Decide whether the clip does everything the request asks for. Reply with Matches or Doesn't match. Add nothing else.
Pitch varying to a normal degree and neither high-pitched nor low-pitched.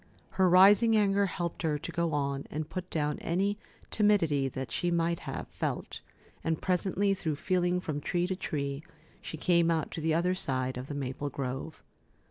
Matches